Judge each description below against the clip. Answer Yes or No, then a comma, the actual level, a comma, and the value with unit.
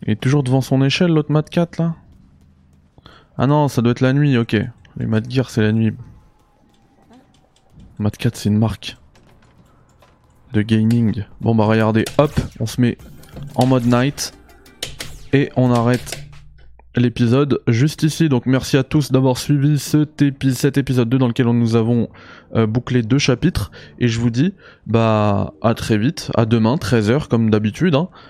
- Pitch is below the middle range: Yes, low, 125 Hz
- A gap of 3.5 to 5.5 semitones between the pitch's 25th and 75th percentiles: Yes, average, 3.8 semitones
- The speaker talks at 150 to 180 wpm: Yes, average, 170 wpm